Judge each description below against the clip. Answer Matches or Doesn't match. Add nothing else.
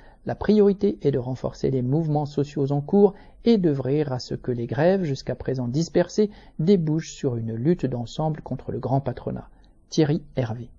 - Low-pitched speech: Doesn't match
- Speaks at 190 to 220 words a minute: Doesn't match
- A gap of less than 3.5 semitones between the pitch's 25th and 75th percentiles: Doesn't match